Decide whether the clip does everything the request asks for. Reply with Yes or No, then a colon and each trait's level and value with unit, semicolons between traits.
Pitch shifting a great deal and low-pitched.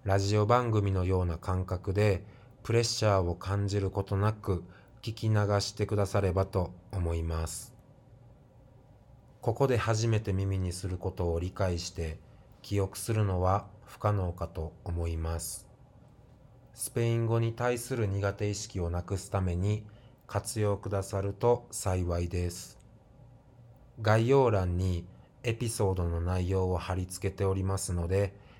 No: average, 3.9 semitones; low, 100 Hz